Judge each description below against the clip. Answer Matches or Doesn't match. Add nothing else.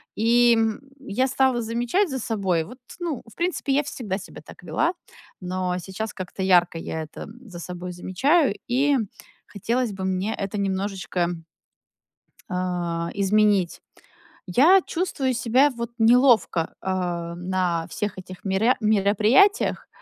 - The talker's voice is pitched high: Matches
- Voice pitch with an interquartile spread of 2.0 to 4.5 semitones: Doesn't match